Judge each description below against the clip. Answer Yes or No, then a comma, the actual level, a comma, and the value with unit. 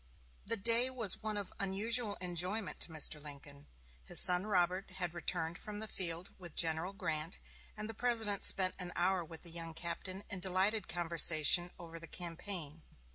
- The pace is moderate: Yes, average, 170 wpm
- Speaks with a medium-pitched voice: Yes, medium, 180 Hz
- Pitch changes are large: No, average, 3.5 semitones